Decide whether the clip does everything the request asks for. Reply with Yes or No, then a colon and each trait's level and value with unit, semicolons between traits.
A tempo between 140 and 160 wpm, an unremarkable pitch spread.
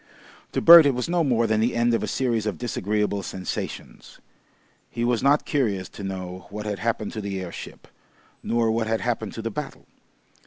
No: average, 195 wpm; average, 3.0 semitones